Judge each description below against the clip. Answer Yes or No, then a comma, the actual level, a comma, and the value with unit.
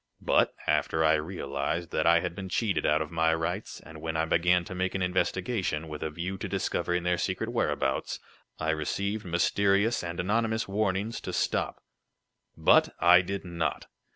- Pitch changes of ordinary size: Yes, average, 3.3 semitones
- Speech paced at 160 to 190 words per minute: Yes, average, 175 wpm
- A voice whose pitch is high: No, very low, 90 Hz